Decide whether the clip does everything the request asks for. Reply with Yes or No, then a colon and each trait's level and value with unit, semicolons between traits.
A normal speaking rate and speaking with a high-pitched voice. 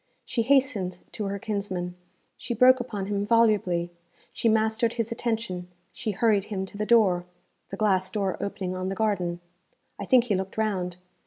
Yes: average, 170 wpm; high, 205 Hz